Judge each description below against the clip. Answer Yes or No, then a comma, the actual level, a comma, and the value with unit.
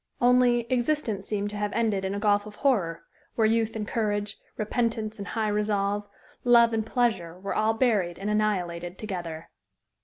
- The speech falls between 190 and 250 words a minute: No, average, 165 wpm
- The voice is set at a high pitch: Yes, high, 210 Hz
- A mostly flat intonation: Yes, narrow, 2.3 semitones